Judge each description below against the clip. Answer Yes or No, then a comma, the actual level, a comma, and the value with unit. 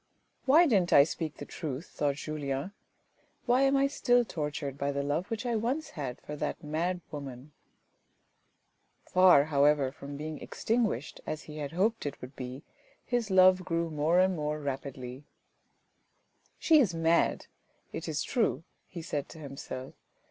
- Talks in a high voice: No, medium, 155 Hz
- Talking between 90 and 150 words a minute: No, average, 170 wpm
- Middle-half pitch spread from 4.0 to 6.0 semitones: Yes, average, 4.8 semitones